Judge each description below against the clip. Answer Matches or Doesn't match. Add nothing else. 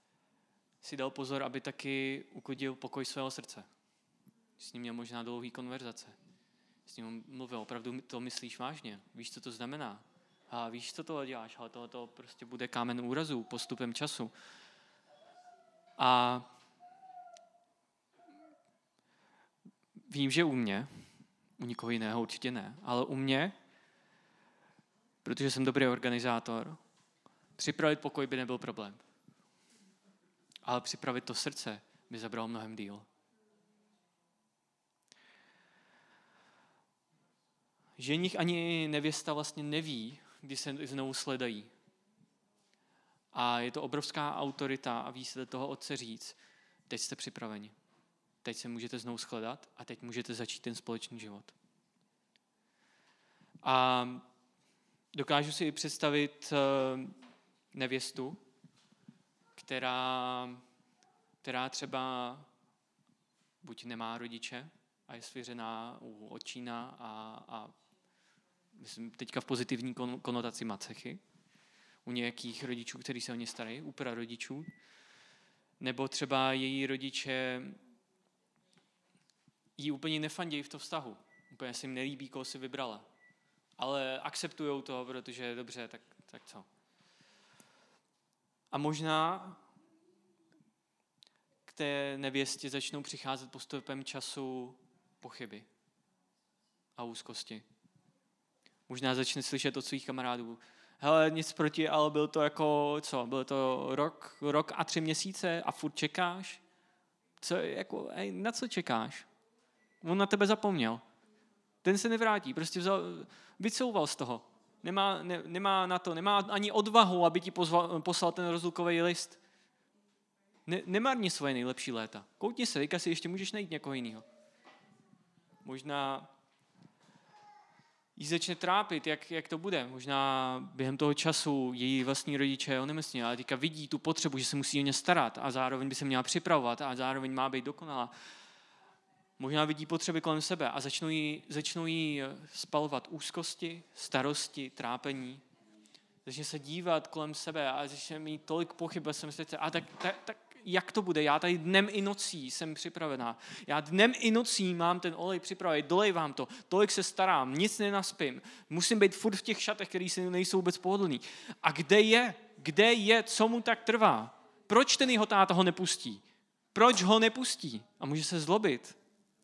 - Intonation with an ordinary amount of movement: Doesn't match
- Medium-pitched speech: Matches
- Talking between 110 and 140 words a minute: Matches